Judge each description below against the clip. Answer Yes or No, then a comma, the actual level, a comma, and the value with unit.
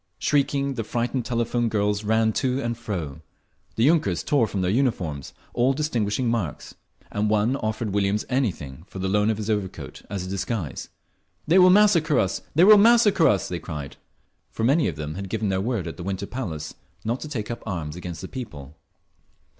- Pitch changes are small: No, wide, 5.4 semitones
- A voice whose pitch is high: No, low, 110 Hz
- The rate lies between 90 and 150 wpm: No, average, 190 wpm